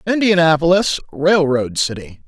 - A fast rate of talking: No, slow, 80 wpm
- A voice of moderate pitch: Yes, medium, 165 Hz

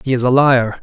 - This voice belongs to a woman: No, male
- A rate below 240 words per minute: No, fast, 290 wpm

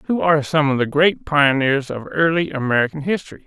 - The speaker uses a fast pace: No, average, 190 wpm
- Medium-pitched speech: Yes, medium, 145 Hz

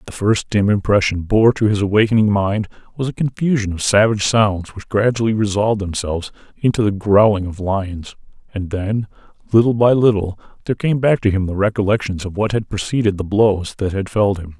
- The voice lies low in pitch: Yes, low, 105 Hz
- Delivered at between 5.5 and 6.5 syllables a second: Yes, 5.8 syllables/s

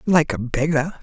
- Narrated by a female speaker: No, male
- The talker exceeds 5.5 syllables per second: No, 4.5 syllables/s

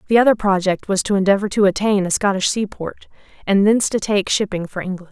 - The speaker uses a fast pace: Yes, fast, 210 wpm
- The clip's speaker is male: No, female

